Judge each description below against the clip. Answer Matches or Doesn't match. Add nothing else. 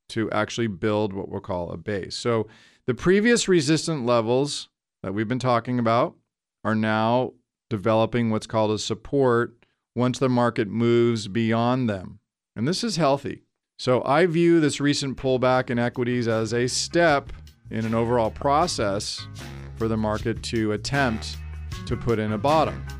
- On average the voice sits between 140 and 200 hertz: Doesn't match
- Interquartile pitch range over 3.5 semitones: Doesn't match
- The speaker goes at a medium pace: Matches